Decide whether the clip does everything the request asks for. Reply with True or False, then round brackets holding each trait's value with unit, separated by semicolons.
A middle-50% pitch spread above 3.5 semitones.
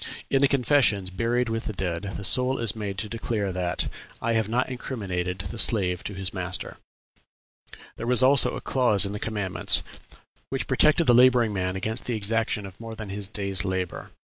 True (4.0 semitones)